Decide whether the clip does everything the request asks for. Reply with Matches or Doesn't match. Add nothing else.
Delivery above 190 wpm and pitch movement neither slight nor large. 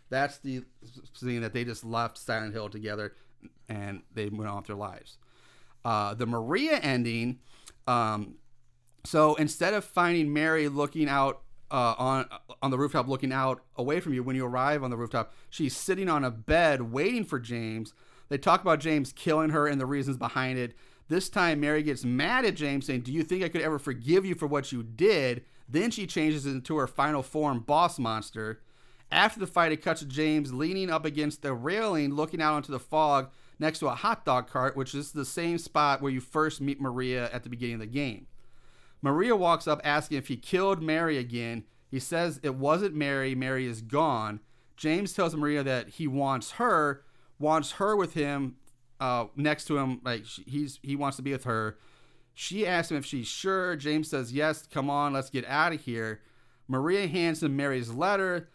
Matches